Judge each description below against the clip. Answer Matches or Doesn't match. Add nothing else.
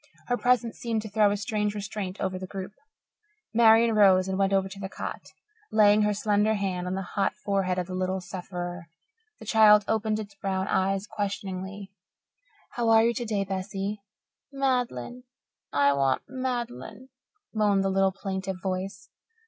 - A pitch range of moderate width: Doesn't match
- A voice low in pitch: Doesn't match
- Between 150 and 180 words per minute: Matches